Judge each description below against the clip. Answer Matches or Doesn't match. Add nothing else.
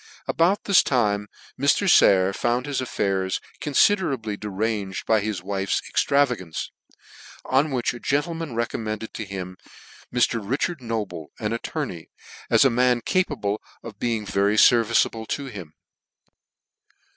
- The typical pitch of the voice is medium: Doesn't match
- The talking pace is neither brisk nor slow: Doesn't match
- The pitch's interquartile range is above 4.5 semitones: Matches